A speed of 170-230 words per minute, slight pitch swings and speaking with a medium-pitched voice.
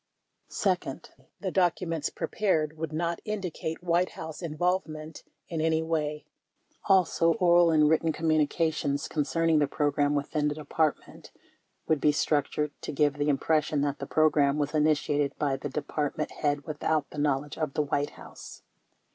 No: average, 150 wpm; narrow, 1.9 semitones; medium, 155 Hz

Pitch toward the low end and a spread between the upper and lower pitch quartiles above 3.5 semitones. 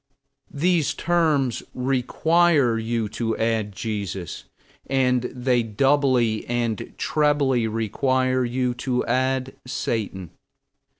No: low, 125 Hz; average, 3.0 semitones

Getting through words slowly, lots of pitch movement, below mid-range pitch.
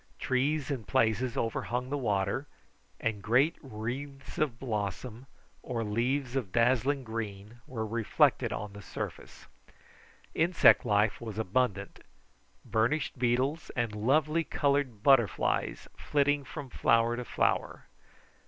No: slow, 115 wpm; average, 4.0 semitones; low, 120 Hz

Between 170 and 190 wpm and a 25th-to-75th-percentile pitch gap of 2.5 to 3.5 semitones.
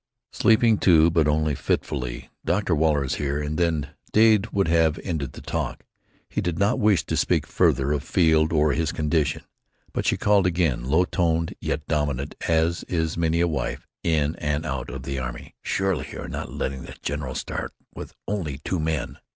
Yes: average, 185 wpm; average, 2.9 semitones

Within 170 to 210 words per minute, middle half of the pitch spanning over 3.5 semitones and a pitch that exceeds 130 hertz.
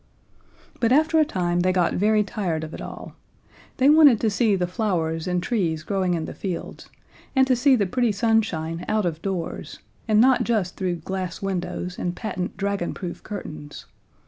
Yes: average, 175 wpm; average, 4.2 semitones; high, 190 Hz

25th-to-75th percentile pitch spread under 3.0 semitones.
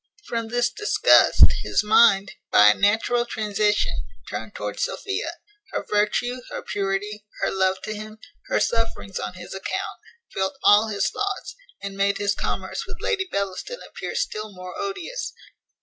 No: average, 3.7 semitones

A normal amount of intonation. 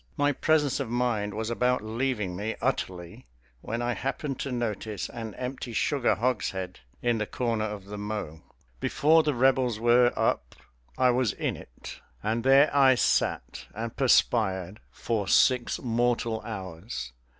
Yes: average, 3.4 semitones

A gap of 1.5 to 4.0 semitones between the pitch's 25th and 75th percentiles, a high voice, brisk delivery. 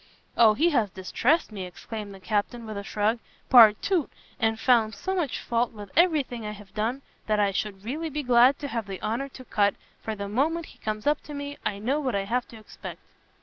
No: average, 4.7 semitones; high, 225 Hz; fast, 225 wpm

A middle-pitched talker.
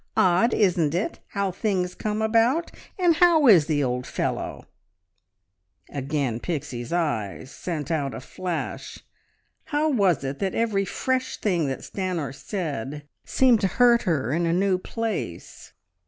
Yes: medium, 180 Hz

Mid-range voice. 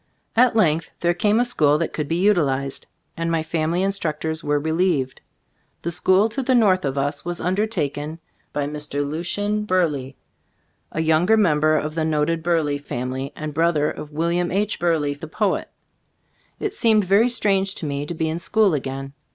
Yes: medium, 165 Hz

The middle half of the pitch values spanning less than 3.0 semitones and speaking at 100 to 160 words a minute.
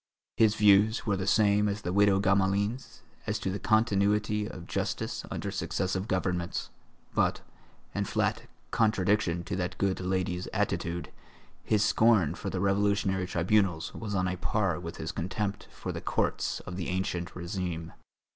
Yes: narrow, 2.5 semitones; average, 155 wpm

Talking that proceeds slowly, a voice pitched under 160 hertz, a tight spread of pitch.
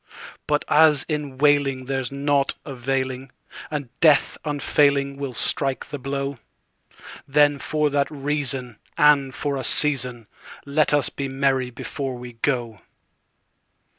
Yes: slow, 110 wpm; medium, 140 Hz; narrow, 1.9 semitones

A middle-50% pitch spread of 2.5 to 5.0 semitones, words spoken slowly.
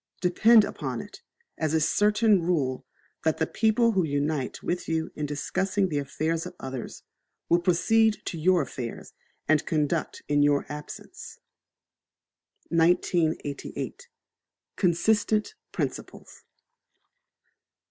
Yes: average, 4.7 semitones; slow, 110 wpm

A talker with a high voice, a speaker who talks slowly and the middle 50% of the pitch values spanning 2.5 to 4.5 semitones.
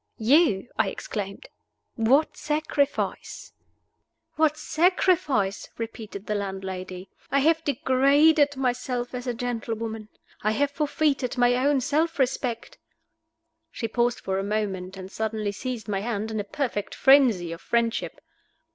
No: high, 240 Hz; slow, 130 wpm; average, 5.2 semitones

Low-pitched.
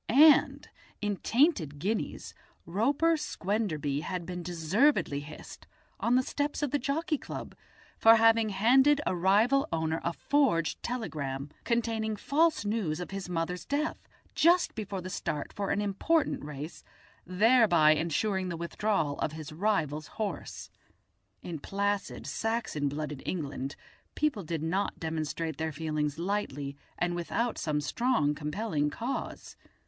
No: high, 190 Hz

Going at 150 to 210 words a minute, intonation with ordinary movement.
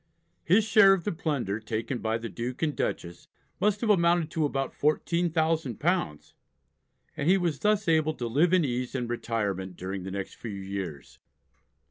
No: average, 165 wpm; wide, 7.7 semitones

